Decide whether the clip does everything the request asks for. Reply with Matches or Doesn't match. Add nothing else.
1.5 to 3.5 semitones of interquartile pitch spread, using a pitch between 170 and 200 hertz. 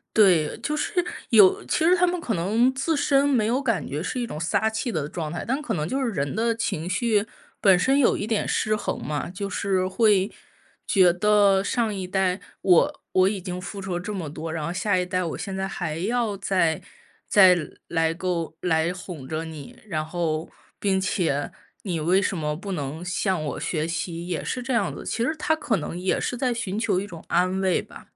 Doesn't match